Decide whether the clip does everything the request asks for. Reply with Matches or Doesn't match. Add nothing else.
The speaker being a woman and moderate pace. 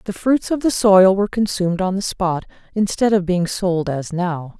Doesn't match